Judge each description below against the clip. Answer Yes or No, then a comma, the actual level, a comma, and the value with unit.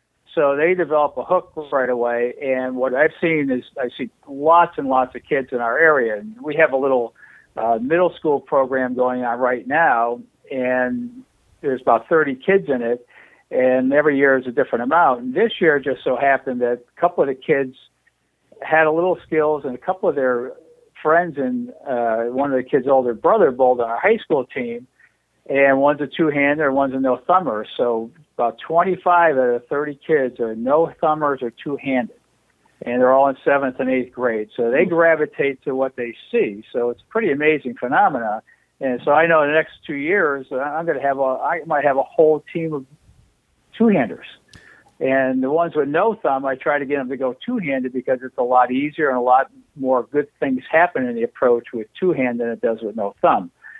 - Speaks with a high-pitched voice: No, low, 135 Hz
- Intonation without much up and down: No, average, 3.8 semitones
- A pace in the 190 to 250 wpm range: Yes, fast, 205 wpm